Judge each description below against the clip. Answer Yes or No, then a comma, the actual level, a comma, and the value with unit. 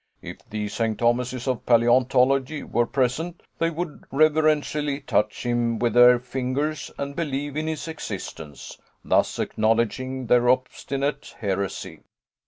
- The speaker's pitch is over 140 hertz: No, low, 130 Hz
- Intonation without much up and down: No, average, 3.6 semitones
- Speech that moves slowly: Yes, slow, 125 wpm